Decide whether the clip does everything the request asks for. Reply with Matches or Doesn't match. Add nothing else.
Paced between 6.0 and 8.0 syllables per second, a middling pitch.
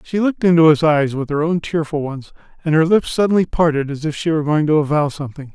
Matches